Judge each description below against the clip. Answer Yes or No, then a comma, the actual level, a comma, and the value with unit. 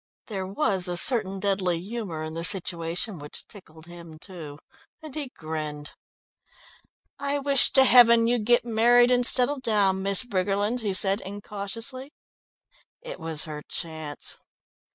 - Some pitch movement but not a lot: No, wide, 6.1 semitones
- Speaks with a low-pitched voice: No, high, 200 Hz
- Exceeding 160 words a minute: No, average, 140 wpm